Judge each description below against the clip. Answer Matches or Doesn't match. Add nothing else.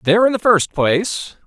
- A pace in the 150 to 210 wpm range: Matches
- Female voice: Doesn't match